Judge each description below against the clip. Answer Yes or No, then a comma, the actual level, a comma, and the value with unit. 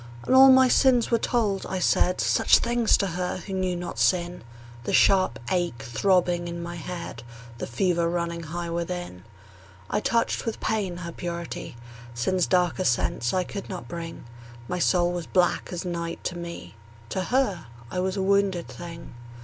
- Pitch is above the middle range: No, medium, 180 Hz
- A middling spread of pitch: No, narrow, 2.0 semitones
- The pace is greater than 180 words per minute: No, average, 175 wpm